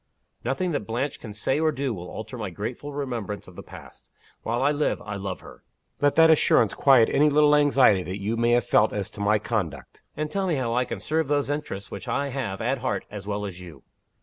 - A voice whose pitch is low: Yes, low, 120 Hz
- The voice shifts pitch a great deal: Yes, wide, 5.9 semitones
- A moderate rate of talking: No, fast, 230 wpm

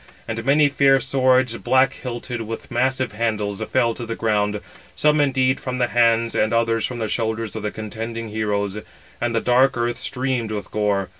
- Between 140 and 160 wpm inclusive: No, average, 180 wpm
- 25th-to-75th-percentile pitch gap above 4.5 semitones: No, average, 2.8 semitones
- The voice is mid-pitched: No, low, 115 Hz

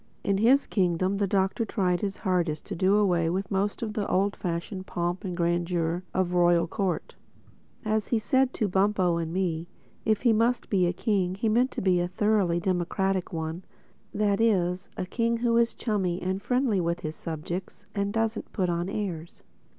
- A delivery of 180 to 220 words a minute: Yes, average, 190 wpm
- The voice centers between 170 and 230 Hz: Yes, high, 190 Hz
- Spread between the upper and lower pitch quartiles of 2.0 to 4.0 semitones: Yes, average, 3.2 semitones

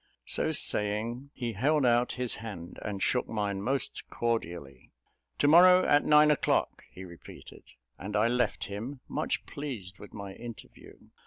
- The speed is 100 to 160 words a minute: Yes, average, 150 wpm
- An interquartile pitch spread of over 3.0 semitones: Yes, average, 5.0 semitones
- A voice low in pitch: Yes, low, 115 Hz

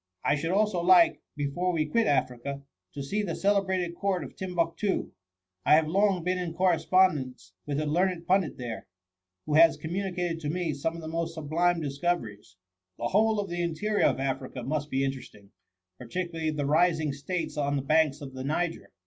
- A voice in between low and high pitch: Yes, medium, 165 Hz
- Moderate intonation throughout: Yes, average, 4.2 semitones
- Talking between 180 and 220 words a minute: Yes, average, 185 wpm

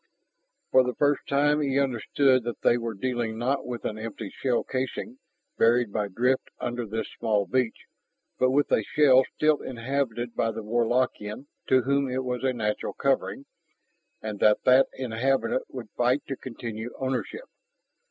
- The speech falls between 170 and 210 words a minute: No, average, 160 wpm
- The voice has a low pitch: Yes, low, 125 Hz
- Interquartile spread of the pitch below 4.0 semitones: Yes, average, 2.8 semitones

